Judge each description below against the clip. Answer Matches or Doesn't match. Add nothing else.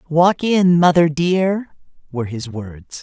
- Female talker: Doesn't match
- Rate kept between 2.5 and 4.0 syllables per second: Matches